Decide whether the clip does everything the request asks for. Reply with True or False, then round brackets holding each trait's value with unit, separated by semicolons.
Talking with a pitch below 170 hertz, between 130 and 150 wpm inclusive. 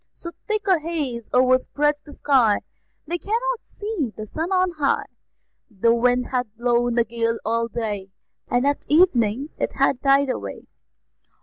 False (255 Hz; 145 wpm)